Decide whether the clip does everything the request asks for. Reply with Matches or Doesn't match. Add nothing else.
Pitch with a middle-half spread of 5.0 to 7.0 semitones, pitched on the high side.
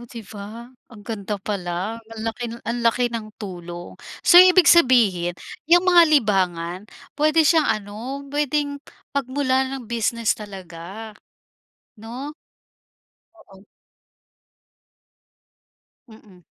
Matches